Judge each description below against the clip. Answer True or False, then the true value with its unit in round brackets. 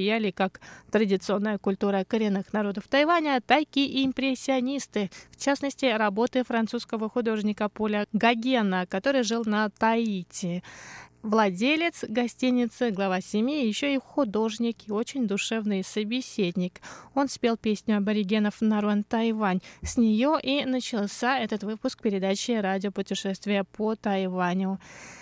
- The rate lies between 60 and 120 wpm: True (115 wpm)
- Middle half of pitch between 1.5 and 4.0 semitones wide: True (3.6 semitones)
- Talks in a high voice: True (220 Hz)